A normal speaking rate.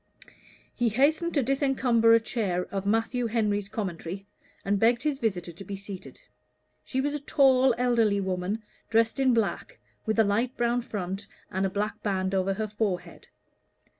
Yes: average, 165 wpm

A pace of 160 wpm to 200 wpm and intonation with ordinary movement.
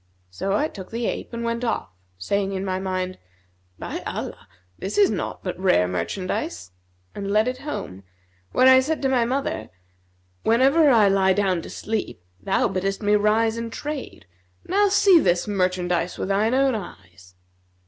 Yes: average, 170 wpm; average, 4.6 semitones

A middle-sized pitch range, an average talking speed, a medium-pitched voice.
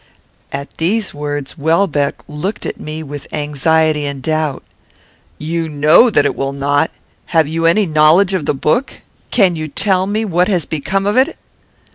Yes: average, 4.3 semitones; average, 165 wpm; medium, 160 Hz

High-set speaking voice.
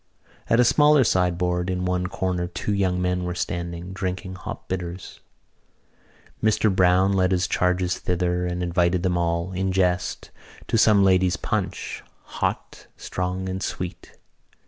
No: very low, 90 Hz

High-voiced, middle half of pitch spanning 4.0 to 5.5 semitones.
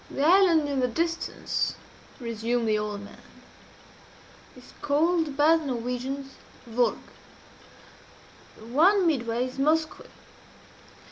Yes: very high, 275 Hz; average, 5.2 semitones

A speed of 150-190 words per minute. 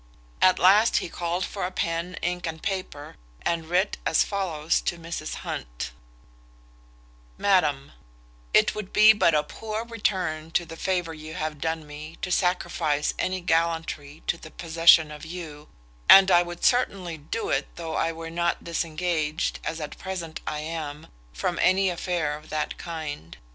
Yes: average, 160 wpm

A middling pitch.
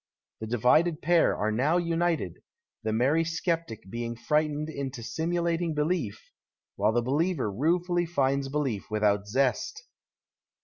Yes: medium, 145 Hz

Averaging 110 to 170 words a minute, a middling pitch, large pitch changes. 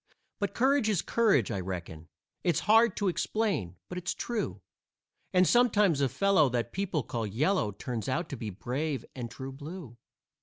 Yes: average, 165 wpm; medium, 155 Hz; wide, 9.0 semitones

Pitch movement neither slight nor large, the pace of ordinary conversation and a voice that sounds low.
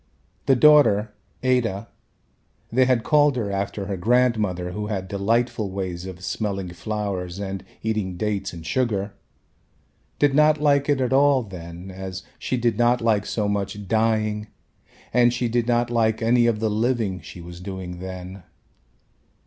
Yes: average, 4.1 semitones; average, 155 wpm; low, 105 Hz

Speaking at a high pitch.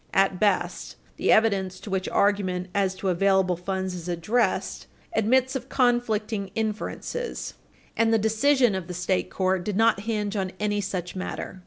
Yes: high, 200 Hz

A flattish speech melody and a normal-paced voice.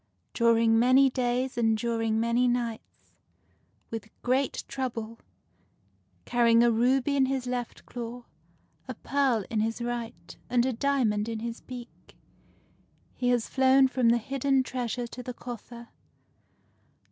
Yes: narrow, 1.8 semitones; average, 145 wpm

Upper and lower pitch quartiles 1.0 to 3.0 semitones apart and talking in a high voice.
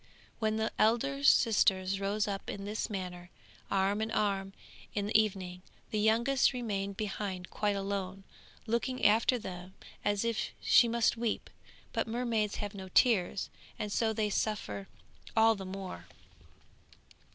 Yes: narrow, 2.4 semitones; high, 210 Hz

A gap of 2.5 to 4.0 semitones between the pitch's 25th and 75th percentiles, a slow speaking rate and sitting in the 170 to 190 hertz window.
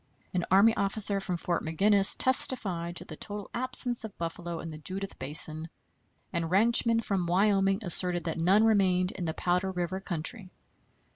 No: average, 3.0 semitones; average, 160 wpm; medium, 185 Hz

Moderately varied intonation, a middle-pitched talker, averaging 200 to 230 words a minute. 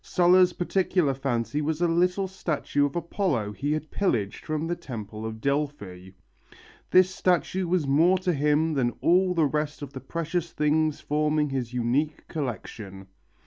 No: average, 4.7 semitones; medium, 150 Hz; average, 155 wpm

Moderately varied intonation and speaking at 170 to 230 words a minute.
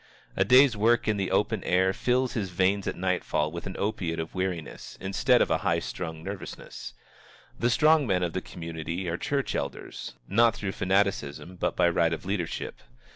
Yes: average, 3.6 semitones; average, 180 wpm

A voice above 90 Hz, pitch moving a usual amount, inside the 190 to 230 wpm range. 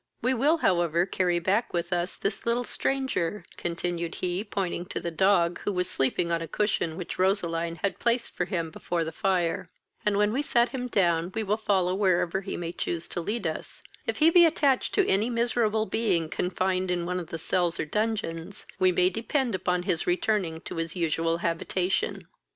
Yes: medium, 185 Hz; average, 3.9 semitones; average, 195 wpm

